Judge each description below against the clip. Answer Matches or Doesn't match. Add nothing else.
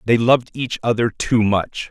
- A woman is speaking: Doesn't match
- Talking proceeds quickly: Doesn't match